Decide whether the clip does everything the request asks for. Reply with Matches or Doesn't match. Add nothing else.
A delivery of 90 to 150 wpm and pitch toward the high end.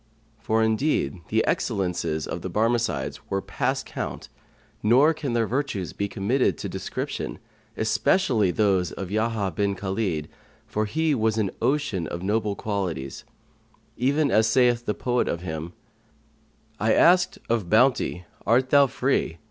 Doesn't match